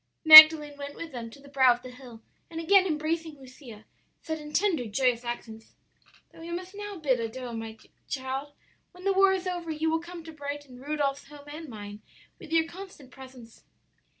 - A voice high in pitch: Yes, very high, 290 Hz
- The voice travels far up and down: No, average, 4.5 semitones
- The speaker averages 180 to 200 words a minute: Yes, average, 190 wpm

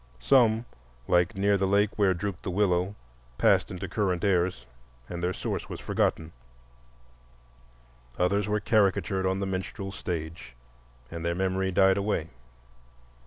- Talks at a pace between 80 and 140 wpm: Yes, slow, 135 wpm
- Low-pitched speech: Yes, very low, 95 Hz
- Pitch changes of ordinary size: No, narrow, 2.2 semitones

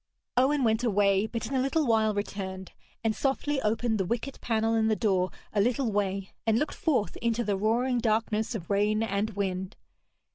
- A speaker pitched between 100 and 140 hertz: No, high, 220 Hz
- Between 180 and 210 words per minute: Yes, average, 185 wpm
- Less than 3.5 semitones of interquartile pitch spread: Yes, average, 2.9 semitones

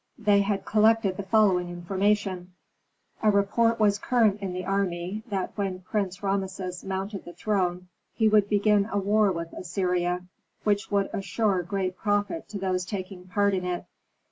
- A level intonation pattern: Yes, narrow, 2.1 semitones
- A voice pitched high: Yes, high, 195 Hz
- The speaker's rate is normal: Yes, average, 160 wpm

